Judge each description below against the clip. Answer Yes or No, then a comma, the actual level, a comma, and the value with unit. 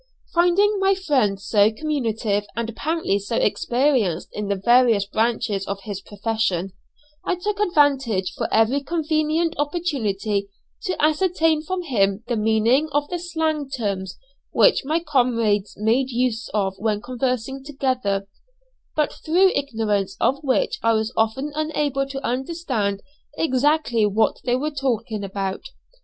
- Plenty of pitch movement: Yes, wide, 6.3 semitones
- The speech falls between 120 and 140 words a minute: Yes, slow, 135 wpm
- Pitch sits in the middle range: No, very high, 250 Hz